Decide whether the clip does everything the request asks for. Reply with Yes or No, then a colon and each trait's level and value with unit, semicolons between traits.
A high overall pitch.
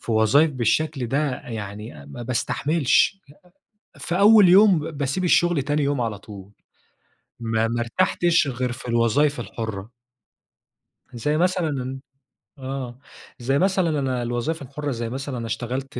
No: low, 130 Hz